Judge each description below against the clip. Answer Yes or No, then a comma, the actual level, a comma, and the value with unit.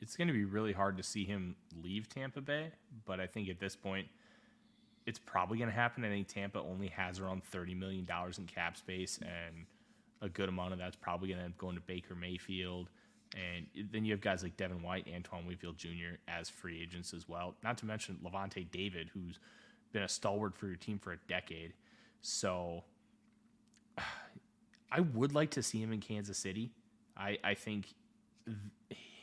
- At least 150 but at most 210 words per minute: Yes, average, 190 wpm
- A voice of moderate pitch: No, very low, 95 Hz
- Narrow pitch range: No, average, 3.3 semitones